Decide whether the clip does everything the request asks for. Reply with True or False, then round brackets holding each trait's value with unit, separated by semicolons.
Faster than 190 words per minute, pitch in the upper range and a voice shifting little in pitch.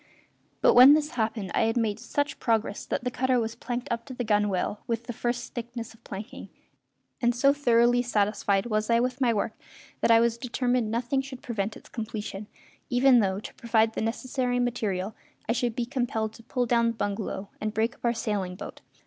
True (200 wpm; 235 Hz; 2.2 semitones)